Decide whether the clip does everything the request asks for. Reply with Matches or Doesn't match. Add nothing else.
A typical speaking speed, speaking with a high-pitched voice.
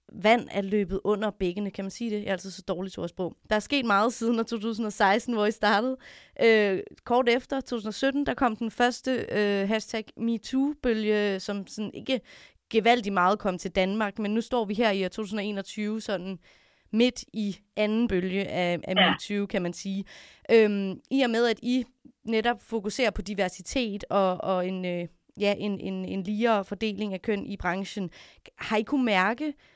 Matches